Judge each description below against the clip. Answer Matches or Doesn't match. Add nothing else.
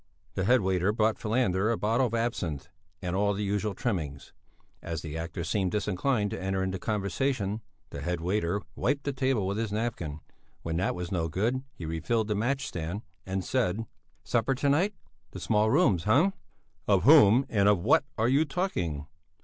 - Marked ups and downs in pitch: Doesn't match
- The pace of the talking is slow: Doesn't match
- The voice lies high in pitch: Doesn't match